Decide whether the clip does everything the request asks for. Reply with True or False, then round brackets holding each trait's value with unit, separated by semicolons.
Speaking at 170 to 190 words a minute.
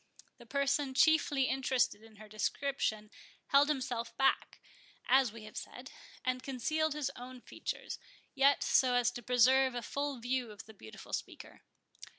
False (155 wpm)